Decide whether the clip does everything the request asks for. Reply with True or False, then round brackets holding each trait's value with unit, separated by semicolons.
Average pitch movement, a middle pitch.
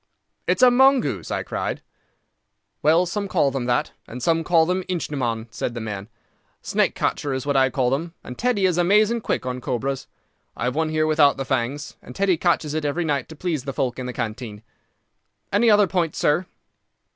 False (5.7 semitones; 150 Hz)